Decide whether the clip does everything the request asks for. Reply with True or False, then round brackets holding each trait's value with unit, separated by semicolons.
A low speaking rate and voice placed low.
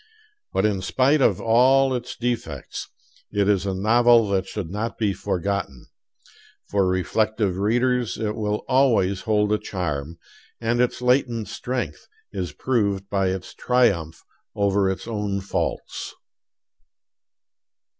True (125 wpm; 105 Hz)